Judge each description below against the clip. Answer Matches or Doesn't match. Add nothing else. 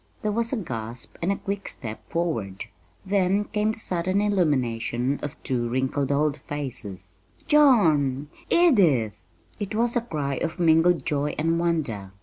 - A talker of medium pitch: Matches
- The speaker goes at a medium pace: Matches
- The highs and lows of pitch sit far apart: Matches